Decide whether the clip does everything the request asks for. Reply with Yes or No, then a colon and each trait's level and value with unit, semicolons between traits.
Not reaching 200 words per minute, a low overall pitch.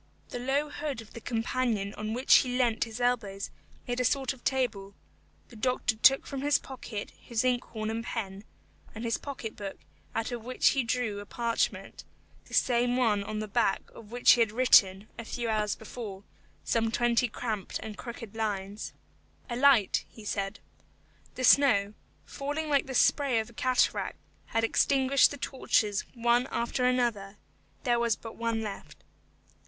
No: average, 170 wpm; high, 235 Hz